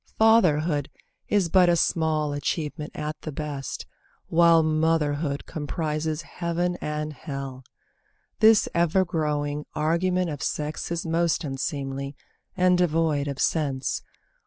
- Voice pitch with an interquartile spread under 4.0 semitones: Yes, narrow, 2.6 semitones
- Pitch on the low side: No, medium, 155 Hz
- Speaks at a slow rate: Yes, slow, 115 wpm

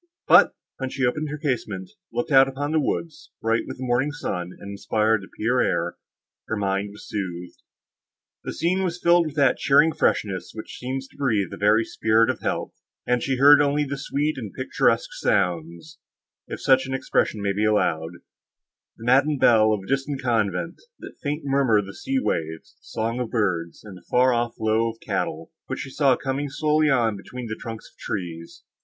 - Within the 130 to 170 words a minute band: No, average, 190 wpm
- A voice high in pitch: No, low, 120 Hz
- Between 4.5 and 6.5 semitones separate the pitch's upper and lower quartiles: Yes, average, 5.3 semitones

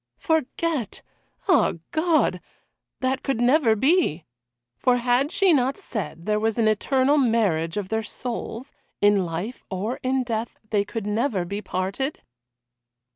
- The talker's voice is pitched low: No, high, 235 Hz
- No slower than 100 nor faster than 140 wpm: Yes, slow, 135 wpm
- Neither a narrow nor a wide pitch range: Yes, average, 4.6 semitones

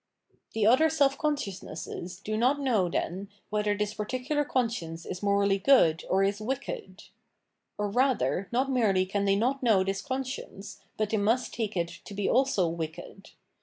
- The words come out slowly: No, average, 165 wpm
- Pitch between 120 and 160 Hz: No, high, 210 Hz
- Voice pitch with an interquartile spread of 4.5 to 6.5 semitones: Yes, average, 4.9 semitones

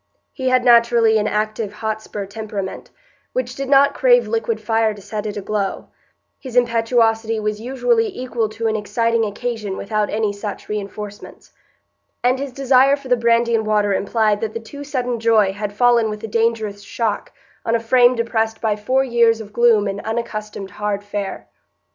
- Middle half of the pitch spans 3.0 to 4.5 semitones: No, narrow, 2.5 semitones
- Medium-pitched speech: No, high, 225 Hz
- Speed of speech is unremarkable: Yes, average, 170 wpm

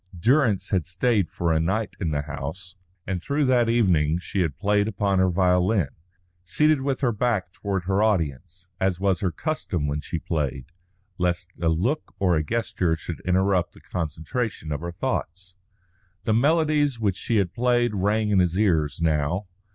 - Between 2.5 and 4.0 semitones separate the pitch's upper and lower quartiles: No, average, 4.7 semitones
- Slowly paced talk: No, average, 175 wpm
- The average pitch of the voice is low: Yes, very low, 95 Hz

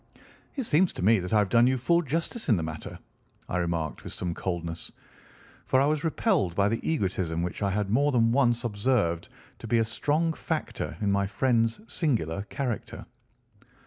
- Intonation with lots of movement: Yes, wide, 6.9 semitones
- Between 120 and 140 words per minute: No, average, 185 wpm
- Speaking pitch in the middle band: No, low, 115 Hz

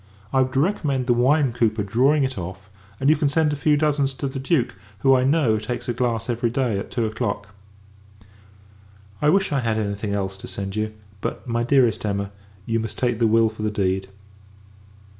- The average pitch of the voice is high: No, low, 120 Hz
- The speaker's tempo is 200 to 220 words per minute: Yes, fast, 205 wpm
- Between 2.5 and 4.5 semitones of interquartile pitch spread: Yes, average, 4.0 semitones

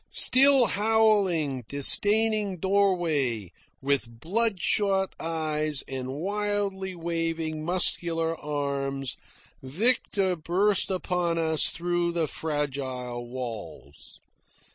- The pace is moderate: No, slow, 85 wpm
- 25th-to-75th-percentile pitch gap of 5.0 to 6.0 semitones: Yes, wide, 5.6 semitones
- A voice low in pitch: No, medium, 165 Hz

